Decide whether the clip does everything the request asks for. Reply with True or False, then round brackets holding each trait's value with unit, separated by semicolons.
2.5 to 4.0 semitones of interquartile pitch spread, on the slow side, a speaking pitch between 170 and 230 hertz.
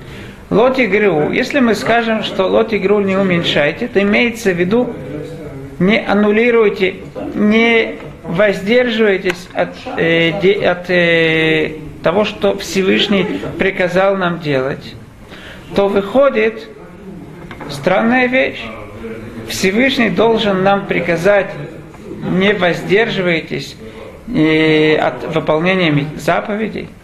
False (4.9 semitones; 90 wpm; 190 Hz)